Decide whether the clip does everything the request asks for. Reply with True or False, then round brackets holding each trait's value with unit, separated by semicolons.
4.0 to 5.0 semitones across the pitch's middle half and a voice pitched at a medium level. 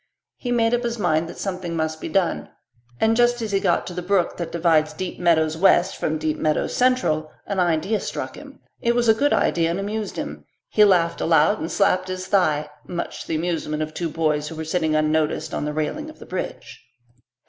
True (4.5 semitones; 175 Hz)